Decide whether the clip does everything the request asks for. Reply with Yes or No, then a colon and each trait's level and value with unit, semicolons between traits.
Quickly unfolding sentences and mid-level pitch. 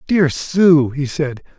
No: average, 150 wpm; medium, 150 Hz